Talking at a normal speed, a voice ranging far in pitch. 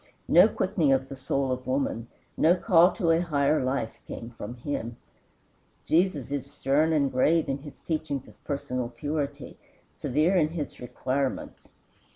No: average, 155 wpm; average, 3.5 semitones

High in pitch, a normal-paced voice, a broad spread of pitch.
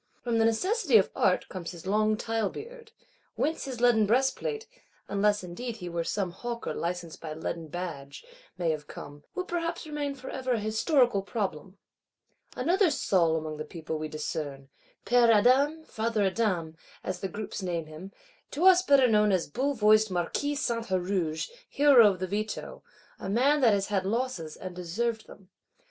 Yes: high, 210 Hz; average, 170 wpm; wide, 6.3 semitones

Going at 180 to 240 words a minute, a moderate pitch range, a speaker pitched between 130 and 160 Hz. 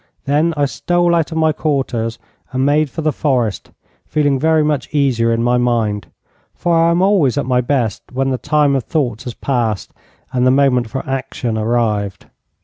Yes: average, 185 wpm; average, 4.1 semitones; low, 135 Hz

